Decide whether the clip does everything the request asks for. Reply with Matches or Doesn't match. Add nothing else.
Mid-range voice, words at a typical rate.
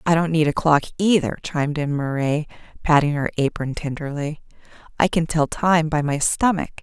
Matches